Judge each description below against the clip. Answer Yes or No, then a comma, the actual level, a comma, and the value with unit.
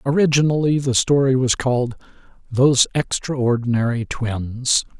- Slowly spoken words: Yes, slow, 95 wpm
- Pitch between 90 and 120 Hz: No, low, 130 Hz